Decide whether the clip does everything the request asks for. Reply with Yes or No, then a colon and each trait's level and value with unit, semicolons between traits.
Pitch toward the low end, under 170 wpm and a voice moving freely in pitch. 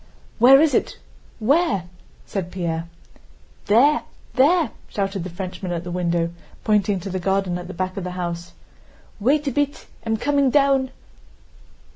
No: high, 195 Hz; average, 145 wpm; wide, 7.2 semitones